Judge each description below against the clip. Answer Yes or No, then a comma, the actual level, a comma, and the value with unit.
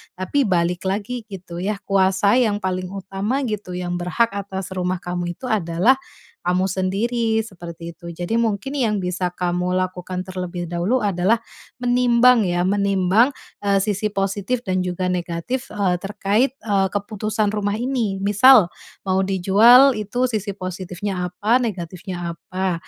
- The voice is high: Yes, high, 195 Hz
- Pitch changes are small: No, average, 3.1 semitones